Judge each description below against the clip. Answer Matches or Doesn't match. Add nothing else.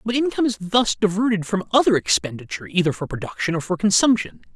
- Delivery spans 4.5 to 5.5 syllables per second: Doesn't match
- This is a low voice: Doesn't match